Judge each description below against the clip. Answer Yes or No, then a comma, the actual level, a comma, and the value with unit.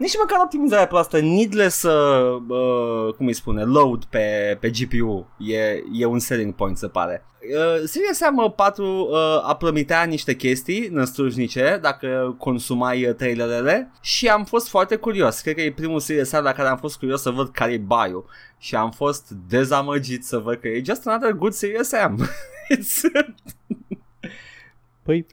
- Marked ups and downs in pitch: Yes, wide, 8.5 semitones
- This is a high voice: No, medium, 140 Hz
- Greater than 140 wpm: Yes, average, 165 wpm